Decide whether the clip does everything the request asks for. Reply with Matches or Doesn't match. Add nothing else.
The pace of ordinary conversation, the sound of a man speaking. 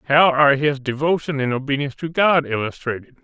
Matches